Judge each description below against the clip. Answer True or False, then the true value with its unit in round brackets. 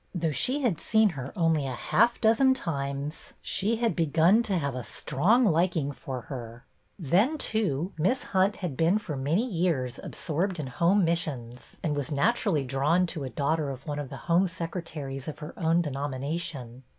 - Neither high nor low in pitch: True (160 Hz)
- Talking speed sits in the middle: True (180 wpm)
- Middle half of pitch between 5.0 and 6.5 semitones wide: True (5.4 semitones)